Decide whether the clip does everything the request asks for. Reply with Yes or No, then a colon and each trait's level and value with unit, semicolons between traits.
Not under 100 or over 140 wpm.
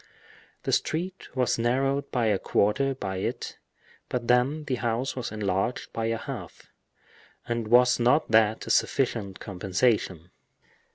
Yes: slow, 135 wpm